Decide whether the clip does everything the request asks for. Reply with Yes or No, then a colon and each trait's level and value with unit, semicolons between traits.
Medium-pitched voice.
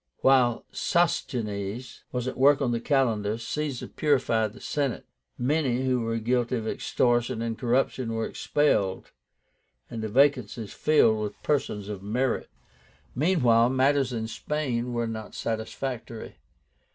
No: low, 120 Hz